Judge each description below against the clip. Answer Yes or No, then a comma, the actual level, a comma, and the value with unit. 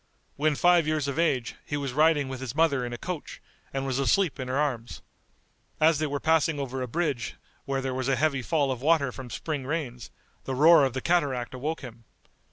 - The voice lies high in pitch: No, medium, 140 Hz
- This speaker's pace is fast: Yes, fast, 215 wpm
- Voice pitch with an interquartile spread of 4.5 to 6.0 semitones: No, average, 3.3 semitones